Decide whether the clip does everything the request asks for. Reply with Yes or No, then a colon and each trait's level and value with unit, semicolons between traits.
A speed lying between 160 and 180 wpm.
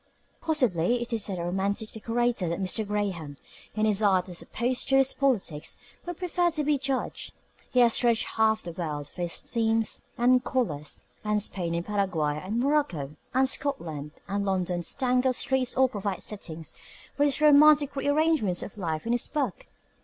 Yes: average, 175 wpm